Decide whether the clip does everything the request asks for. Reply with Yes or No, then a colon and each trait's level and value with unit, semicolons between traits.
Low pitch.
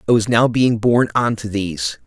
Yes: low, 115 Hz